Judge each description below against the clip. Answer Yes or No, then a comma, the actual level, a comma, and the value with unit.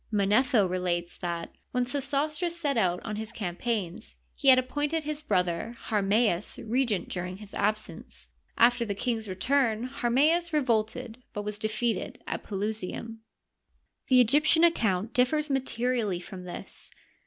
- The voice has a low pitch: No, high, 225 Hz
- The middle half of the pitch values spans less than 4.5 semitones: No, average, 5.1 semitones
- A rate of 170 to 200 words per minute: No, slow, 135 wpm